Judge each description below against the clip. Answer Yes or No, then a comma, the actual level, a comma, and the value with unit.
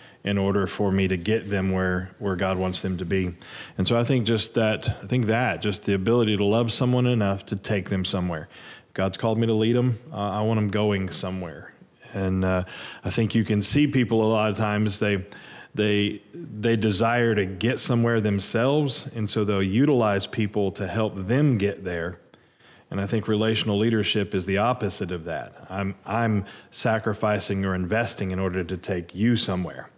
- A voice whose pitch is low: Yes, low, 105 Hz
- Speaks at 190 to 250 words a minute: Yes, average, 195 wpm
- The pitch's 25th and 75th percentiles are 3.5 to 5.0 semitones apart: No, average, 2.8 semitones